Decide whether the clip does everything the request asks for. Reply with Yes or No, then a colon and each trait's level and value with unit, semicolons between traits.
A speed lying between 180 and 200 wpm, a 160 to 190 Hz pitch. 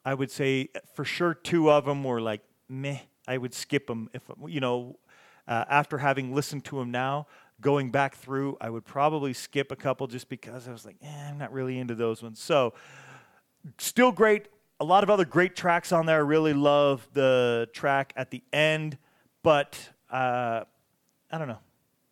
No: average, 190 wpm; medium, 140 Hz